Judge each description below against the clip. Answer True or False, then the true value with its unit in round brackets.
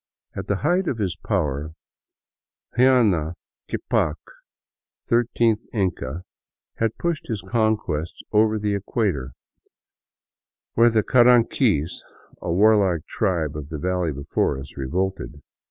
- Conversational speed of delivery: False (120 wpm)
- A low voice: True (100 Hz)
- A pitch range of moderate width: False (6.3 semitones)